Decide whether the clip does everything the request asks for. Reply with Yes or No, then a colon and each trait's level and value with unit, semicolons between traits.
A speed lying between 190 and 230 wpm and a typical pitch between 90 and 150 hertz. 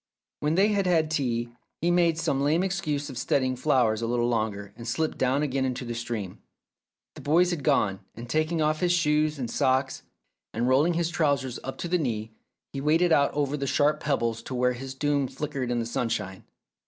Yes: fast, 205 wpm; medium, 140 Hz